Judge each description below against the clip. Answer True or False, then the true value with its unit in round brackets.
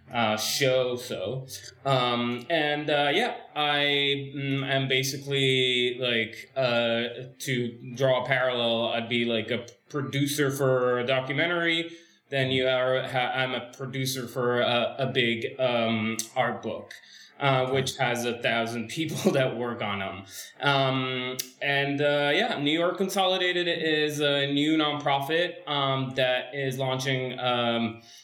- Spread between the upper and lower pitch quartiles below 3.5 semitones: True (2.7 semitones)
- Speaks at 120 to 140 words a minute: True (135 wpm)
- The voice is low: True (130 Hz)